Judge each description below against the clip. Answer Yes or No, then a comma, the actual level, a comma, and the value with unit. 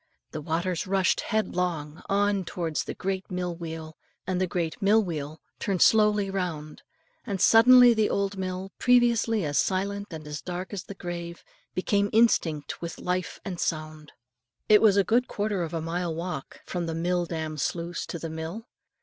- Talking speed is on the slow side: No, average, 170 wpm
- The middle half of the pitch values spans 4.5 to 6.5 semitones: No, average, 3.5 semitones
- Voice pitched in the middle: Yes, medium, 180 Hz